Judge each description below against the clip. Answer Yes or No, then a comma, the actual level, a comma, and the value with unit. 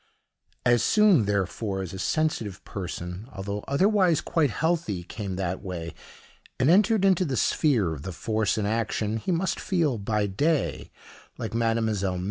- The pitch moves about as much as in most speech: No, wide, 8.4 semitones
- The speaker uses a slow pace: No, average, 150 wpm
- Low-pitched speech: Yes, low, 110 Hz